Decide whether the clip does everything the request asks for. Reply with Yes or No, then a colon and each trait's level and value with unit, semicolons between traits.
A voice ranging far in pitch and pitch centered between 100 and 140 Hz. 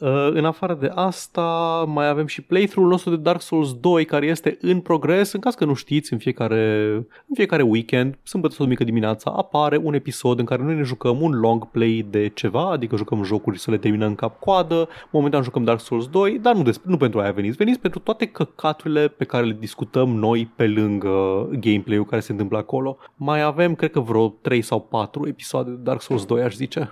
Yes: wide, 6.3 semitones; low, 135 Hz